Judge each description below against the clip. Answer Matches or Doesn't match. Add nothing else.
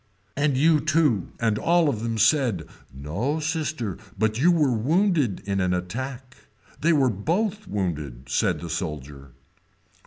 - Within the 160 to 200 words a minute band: Doesn't match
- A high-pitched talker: Doesn't match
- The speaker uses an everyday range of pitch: Doesn't match